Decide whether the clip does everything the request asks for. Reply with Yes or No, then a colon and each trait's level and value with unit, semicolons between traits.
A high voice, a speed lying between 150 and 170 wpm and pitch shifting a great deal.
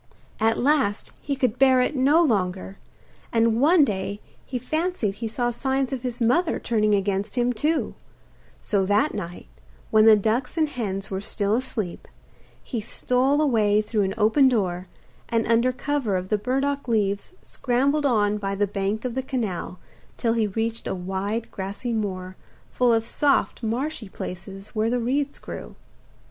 No: high, 230 Hz; average, 165 wpm; average, 4.3 semitones